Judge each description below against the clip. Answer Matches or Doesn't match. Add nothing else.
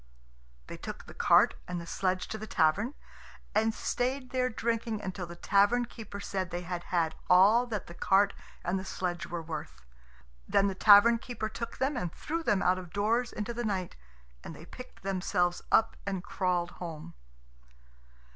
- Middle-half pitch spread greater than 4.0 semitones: Matches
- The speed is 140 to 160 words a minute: Doesn't match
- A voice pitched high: Matches